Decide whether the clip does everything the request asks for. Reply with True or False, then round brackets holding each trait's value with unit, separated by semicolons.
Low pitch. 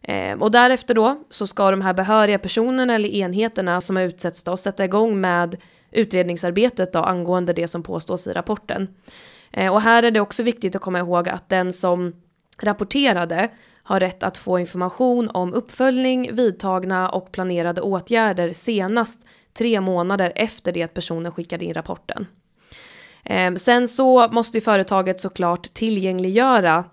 False (195 Hz)